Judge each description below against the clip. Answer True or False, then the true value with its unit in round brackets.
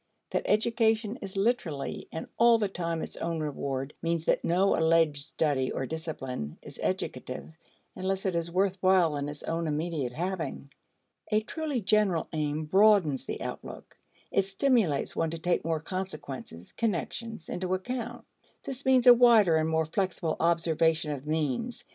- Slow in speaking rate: False (155 wpm)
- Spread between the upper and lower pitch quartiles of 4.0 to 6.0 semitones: True (4.7 semitones)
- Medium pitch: True (170 Hz)